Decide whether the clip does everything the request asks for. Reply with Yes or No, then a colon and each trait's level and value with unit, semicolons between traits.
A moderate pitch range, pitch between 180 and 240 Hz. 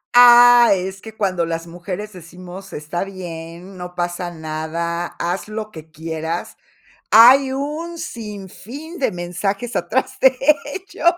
No: wide, 5.8 semitones; high, 190 Hz